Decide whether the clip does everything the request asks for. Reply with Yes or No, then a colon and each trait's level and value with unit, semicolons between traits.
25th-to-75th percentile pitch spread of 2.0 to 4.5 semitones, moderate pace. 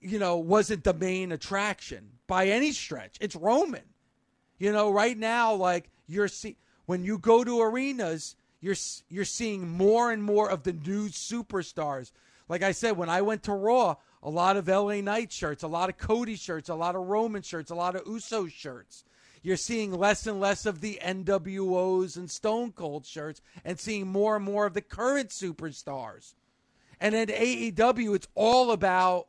Yes: average, 3.5 semitones; average, 185 wpm